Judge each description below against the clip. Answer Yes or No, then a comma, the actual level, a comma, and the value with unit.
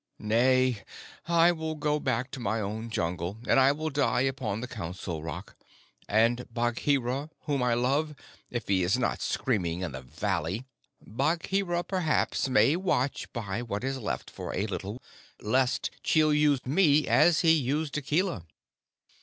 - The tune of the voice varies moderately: No, wide, 5.8 semitones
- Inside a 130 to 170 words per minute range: Yes, average, 155 wpm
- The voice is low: Yes, low, 125 Hz